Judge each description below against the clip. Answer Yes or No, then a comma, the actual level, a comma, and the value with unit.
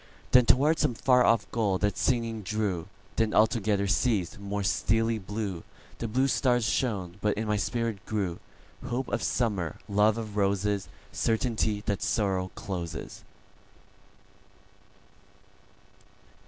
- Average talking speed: No, slow, 110 wpm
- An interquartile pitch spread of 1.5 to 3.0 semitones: Yes, average, 2.7 semitones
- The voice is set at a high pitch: No, low, 105 Hz